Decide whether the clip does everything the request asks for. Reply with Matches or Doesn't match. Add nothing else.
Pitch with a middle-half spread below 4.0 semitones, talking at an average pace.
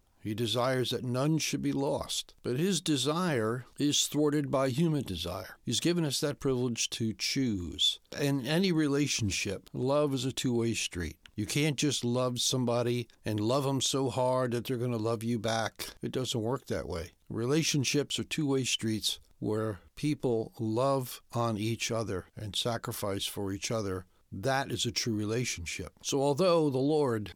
Doesn't match